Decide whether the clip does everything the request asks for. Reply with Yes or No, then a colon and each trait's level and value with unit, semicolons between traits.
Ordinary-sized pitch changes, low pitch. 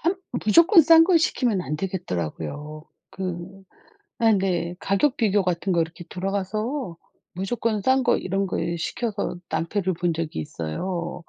No: average, 4.6 semitones; high, 190 Hz